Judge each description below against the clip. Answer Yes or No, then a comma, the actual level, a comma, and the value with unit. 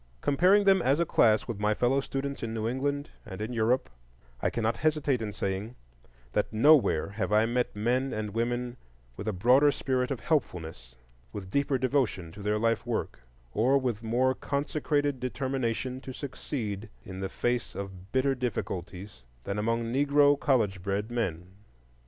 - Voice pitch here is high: No, low, 120 Hz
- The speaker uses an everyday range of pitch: Yes, average, 4.5 semitones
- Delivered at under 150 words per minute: No, average, 165 wpm